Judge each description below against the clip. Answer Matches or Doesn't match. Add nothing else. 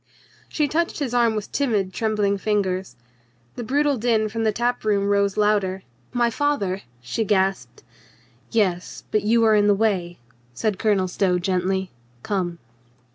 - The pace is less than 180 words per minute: Matches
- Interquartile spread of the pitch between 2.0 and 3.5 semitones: Matches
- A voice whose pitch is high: Matches